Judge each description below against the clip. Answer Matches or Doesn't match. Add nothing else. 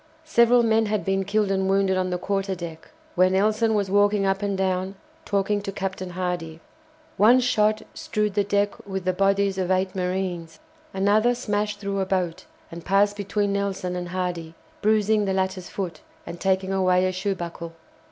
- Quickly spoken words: Doesn't match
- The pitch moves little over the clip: Matches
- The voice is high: Matches